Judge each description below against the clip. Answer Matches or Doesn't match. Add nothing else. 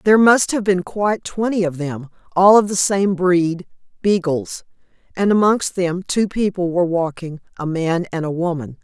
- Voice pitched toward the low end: Doesn't match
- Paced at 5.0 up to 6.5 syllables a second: Doesn't match